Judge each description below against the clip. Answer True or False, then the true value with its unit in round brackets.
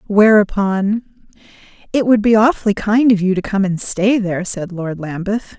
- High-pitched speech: True (205 Hz)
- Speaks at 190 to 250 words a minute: False (160 wpm)